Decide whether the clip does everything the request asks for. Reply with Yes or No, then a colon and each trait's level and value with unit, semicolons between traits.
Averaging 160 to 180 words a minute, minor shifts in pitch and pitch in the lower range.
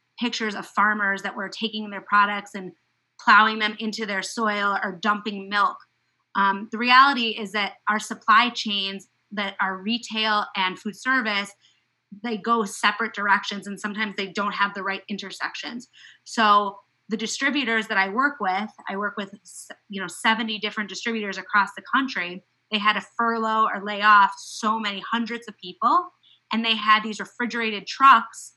No: average, 165 wpm; narrow, 2.0 semitones; high, 210 Hz